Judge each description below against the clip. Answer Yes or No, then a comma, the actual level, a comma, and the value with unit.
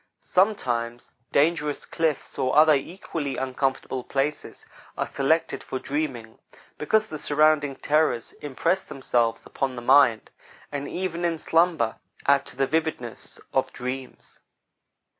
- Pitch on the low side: No, medium, 145 Hz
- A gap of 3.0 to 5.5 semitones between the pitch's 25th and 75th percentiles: Yes, average, 3.5 semitones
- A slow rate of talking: Yes, slow, 120 wpm